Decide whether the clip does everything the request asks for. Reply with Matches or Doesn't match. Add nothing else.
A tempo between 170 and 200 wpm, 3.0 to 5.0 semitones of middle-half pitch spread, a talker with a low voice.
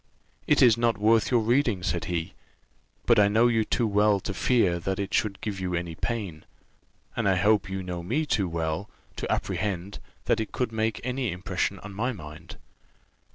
Matches